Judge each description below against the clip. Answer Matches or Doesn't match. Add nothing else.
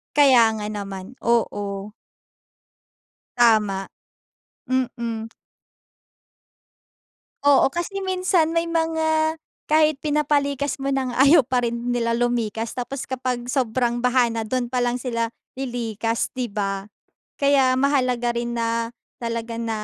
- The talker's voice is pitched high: Matches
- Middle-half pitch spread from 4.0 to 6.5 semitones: Doesn't match